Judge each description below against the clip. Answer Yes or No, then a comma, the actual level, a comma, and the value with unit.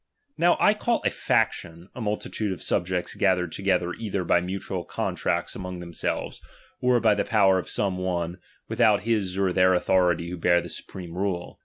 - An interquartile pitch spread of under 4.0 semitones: Yes, average, 2.7 semitones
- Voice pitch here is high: No, very low, 95 Hz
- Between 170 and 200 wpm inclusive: Yes, average, 180 wpm